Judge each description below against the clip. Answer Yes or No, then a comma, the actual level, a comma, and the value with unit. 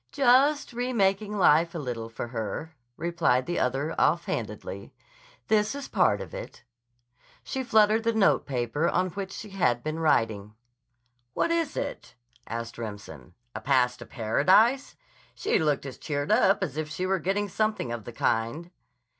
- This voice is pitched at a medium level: Yes, medium, 170 Hz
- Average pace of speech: Yes, average, 155 wpm